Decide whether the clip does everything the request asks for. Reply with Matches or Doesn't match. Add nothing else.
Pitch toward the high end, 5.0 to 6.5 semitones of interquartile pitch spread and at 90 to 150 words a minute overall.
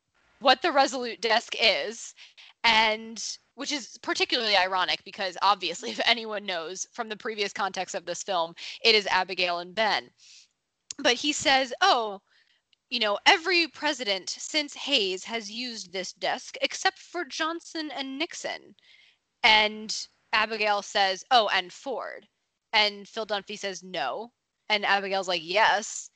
Matches